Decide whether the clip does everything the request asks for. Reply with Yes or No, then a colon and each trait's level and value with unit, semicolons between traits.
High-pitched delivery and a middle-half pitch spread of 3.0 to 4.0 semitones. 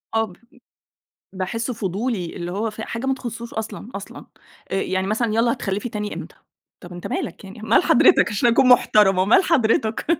Yes: high, 220 Hz; average, 3.4 semitones